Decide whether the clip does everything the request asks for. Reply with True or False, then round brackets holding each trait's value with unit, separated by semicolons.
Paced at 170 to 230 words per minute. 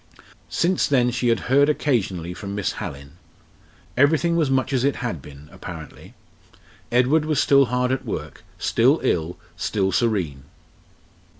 False (140 wpm)